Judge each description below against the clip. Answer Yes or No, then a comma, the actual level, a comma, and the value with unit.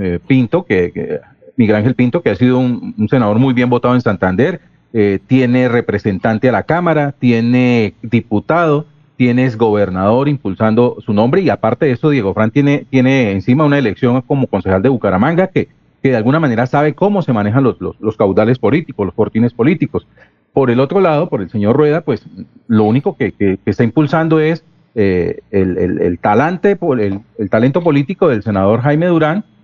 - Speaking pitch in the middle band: No, low, 125 Hz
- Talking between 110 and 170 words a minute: No, average, 185 wpm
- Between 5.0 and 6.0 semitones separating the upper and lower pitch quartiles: Yes, average, 5.3 semitones